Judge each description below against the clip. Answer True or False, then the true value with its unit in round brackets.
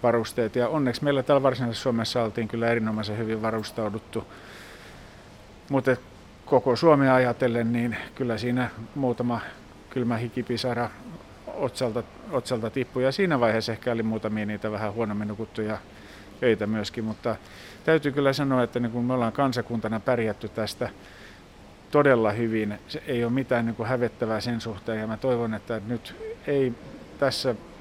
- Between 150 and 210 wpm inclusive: False (140 wpm)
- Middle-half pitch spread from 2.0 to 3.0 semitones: True (2.4 semitones)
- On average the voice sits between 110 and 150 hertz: True (115 Hz)